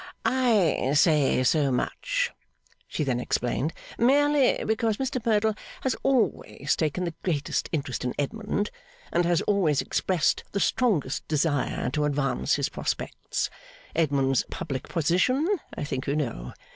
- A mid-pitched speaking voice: Yes, medium, 165 Hz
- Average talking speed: No, slow, 130 wpm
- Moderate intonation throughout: No, wide, 7.9 semitones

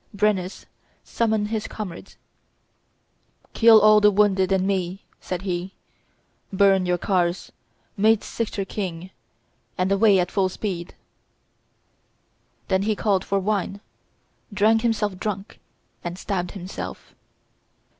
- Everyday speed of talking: No, slow, 115 wpm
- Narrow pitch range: Yes, narrow, 2.2 semitones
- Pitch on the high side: Yes, high, 195 Hz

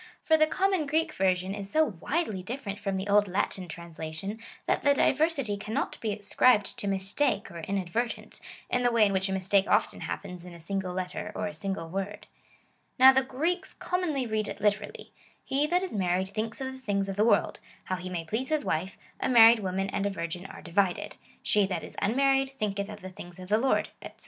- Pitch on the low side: No, high, 205 Hz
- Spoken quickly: Yes, fast, 215 wpm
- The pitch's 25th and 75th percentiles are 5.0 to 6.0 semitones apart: Yes, wide, 5.6 semitones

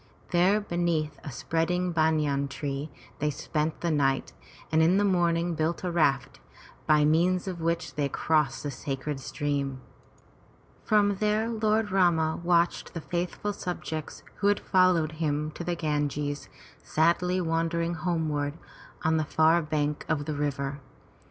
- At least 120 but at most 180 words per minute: Yes, average, 140 wpm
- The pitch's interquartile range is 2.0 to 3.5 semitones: Yes, average, 3.0 semitones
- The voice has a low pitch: No, medium, 160 Hz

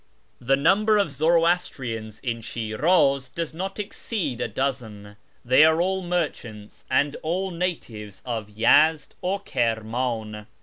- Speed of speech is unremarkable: No, slow, 125 wpm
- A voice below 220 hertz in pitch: Yes, medium, 140 Hz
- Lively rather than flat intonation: Yes, wide, 7.4 semitones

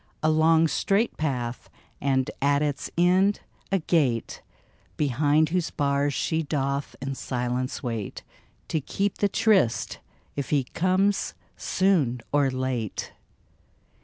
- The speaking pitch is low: No, medium, 145 Hz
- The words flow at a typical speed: No, slow, 125 wpm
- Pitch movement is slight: No, average, 4.4 semitones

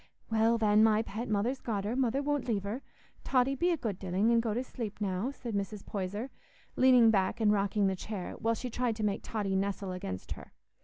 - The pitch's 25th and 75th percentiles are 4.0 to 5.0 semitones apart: No, average, 3.2 semitones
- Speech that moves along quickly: Yes, fast, 215 wpm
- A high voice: Yes, high, 220 Hz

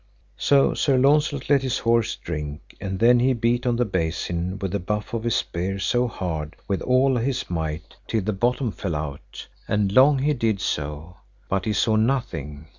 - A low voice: Yes, low, 105 Hz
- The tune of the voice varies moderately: No, wide, 6.1 semitones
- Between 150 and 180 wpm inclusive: No, average, 190 wpm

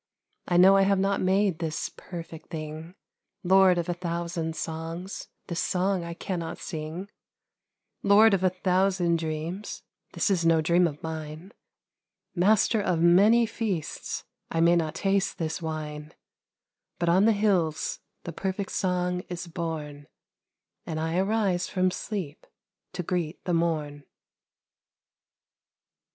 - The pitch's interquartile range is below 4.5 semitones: Yes, average, 2.8 semitones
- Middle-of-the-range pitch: Yes, medium, 175 Hz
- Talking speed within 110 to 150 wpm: Yes, slow, 135 wpm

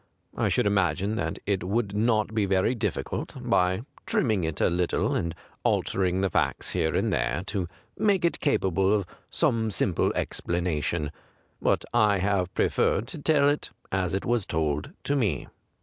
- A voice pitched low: Yes, low, 100 Hz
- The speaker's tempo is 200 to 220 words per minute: No, average, 165 wpm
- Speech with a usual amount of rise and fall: Yes, average, 3.9 semitones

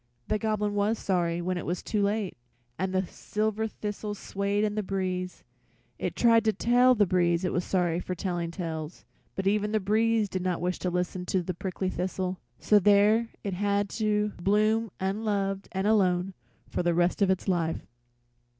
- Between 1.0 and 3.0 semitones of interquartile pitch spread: Yes, narrow, 2.6 semitones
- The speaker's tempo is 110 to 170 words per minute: No, average, 180 wpm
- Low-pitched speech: No, high, 195 Hz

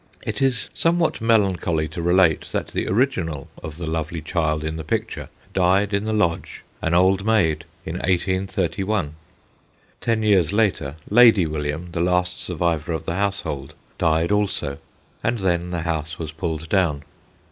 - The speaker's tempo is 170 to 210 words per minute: No, average, 155 wpm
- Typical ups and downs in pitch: Yes, average, 3.9 semitones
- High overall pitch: No, very low, 85 Hz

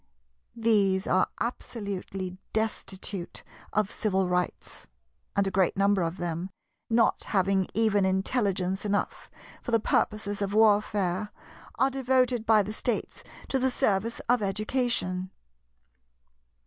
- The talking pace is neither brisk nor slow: No, slow, 120 wpm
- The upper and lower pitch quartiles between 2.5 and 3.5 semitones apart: Yes, average, 2.9 semitones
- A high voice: Yes, high, 205 Hz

